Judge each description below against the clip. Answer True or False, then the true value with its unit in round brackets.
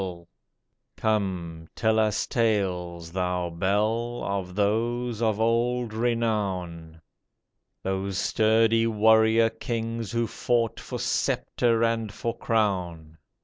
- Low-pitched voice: True (110 Hz)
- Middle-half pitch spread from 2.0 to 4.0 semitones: True (3.7 semitones)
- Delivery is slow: True (105 wpm)